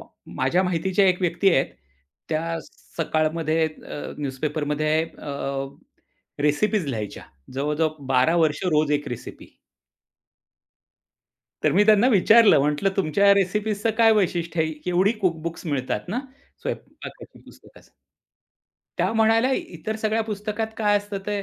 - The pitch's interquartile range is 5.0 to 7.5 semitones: Yes, average, 5.3 semitones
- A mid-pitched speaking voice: Yes, medium, 170 Hz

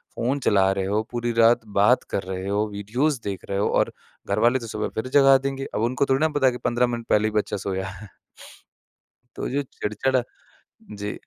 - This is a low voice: Yes, low, 115 Hz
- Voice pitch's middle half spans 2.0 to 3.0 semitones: No, average, 4.2 semitones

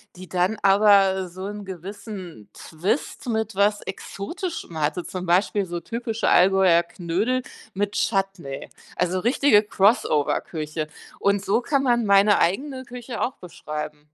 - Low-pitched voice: No, high, 195 Hz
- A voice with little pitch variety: No, average, 3.8 semitones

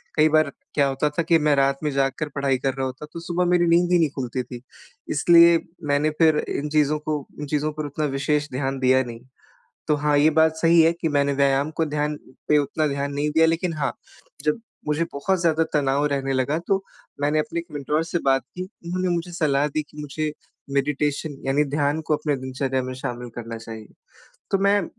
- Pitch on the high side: No, medium, 150 Hz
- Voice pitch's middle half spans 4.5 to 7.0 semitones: No, average, 2.7 semitones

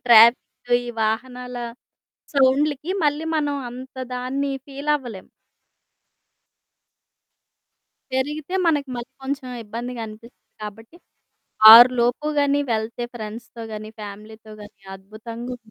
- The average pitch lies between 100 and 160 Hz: No, high, 245 Hz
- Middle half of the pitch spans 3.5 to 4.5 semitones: Yes, average, 3.9 semitones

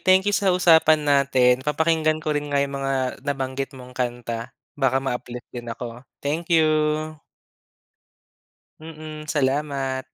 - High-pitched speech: No, medium, 140 Hz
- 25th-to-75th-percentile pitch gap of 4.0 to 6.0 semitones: No, average, 3.3 semitones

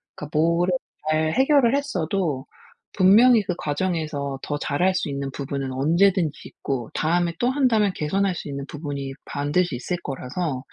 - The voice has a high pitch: No, medium, 155 Hz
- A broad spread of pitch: No, average, 5.0 semitones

